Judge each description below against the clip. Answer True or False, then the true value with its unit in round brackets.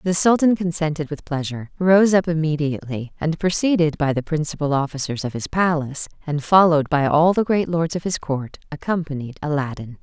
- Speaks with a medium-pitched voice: True (155 Hz)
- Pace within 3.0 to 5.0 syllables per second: False (5.6 syllables/s)